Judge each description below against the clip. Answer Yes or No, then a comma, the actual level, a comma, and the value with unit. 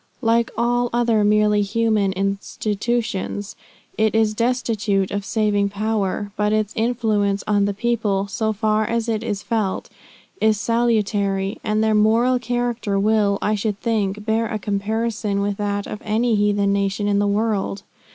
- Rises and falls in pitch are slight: Yes, narrow, 2.0 semitones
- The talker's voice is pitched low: No, high, 210 Hz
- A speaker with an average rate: Yes, average, 150 wpm